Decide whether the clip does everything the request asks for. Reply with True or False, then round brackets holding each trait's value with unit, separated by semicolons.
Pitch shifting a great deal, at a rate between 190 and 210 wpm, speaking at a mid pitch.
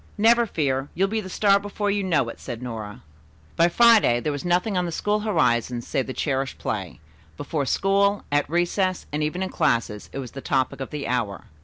True (7.2 semitones; 205 wpm; 155 Hz)